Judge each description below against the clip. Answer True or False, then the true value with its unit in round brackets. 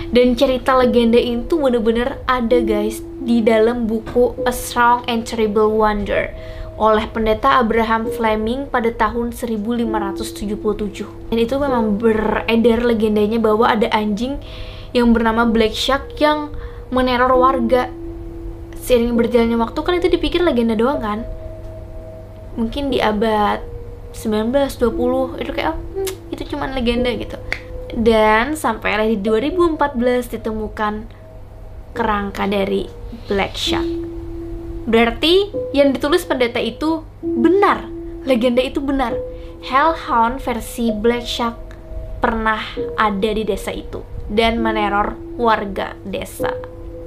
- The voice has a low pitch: False (230 Hz)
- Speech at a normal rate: True (110 wpm)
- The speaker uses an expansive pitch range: False (3.4 semitones)